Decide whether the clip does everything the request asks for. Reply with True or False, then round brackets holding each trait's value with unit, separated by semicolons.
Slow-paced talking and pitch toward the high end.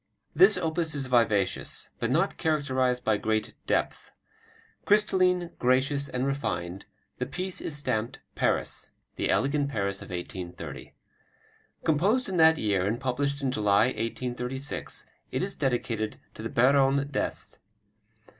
False (130 wpm; 130 Hz)